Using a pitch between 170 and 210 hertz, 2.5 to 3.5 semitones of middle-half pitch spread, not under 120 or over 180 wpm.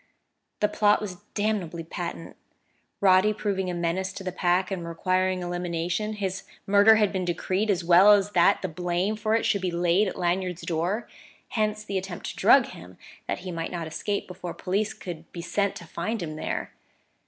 No: medium, 185 Hz; average, 2.9 semitones; average, 190 wpm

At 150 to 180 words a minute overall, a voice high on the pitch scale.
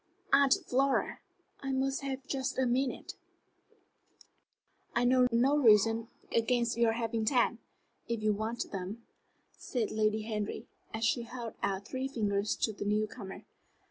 No: average, 140 wpm; high, 235 Hz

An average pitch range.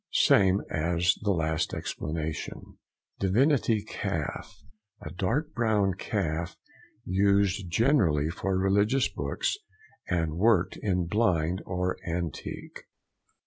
Yes: average, 3.9 semitones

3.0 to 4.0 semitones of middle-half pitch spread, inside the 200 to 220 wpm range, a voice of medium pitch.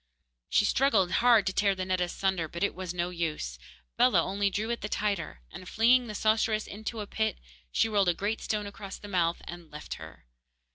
No: average, 3.5 semitones; fast, 205 wpm; high, 195 Hz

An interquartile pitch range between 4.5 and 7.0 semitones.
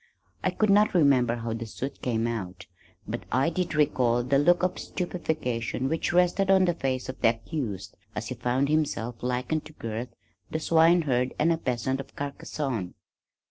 Yes: average, 5.3 semitones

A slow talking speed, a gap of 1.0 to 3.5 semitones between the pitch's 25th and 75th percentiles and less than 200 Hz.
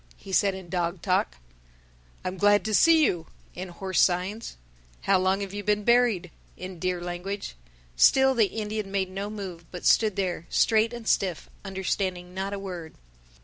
No: average, 175 wpm; narrow, 2.4 semitones; high, 190 Hz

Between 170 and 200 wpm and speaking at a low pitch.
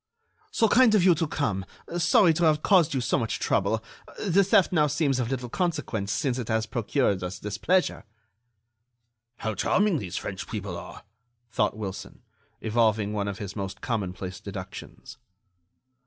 No: average, 155 wpm; low, 120 Hz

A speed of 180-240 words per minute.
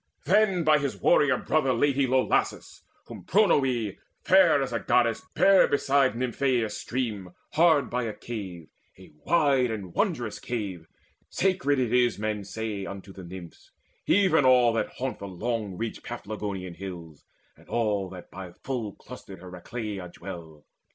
No: average, 150 wpm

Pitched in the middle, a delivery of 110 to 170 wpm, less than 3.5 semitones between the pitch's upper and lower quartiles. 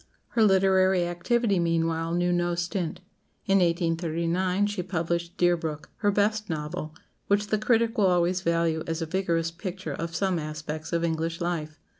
Yes: medium, 175 Hz; average, 155 wpm; narrow, 2.5 semitones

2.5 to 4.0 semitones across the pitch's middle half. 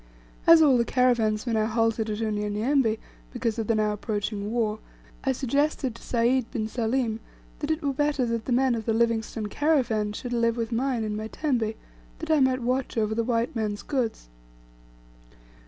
Yes: average, 3.1 semitones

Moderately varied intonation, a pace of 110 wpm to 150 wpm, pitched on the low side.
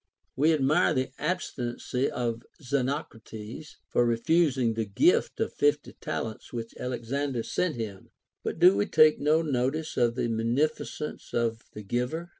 Yes: average, 4.8 semitones; average, 140 wpm; low, 130 Hz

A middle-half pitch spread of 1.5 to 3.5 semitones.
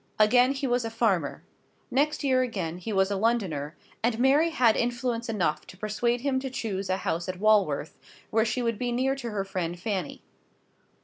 No: average, 4.5 semitones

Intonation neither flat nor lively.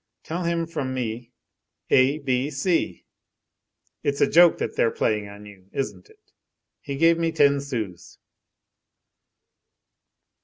No: wide, 6.4 semitones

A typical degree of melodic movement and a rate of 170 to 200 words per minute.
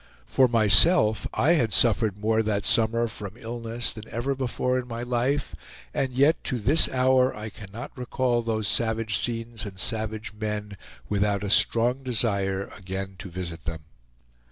No: average, 3.0 semitones; average, 155 wpm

